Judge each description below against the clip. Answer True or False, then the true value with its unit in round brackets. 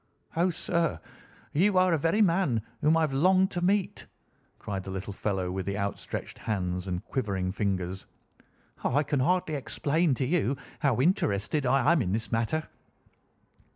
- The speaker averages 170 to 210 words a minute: False (155 wpm)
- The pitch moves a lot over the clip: True (8.9 semitones)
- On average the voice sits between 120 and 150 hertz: True (135 Hz)